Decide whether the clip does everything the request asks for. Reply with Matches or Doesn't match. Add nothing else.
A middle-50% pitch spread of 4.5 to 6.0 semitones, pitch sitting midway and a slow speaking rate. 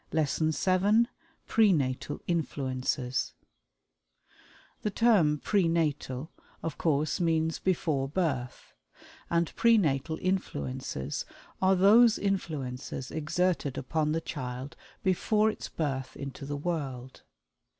Matches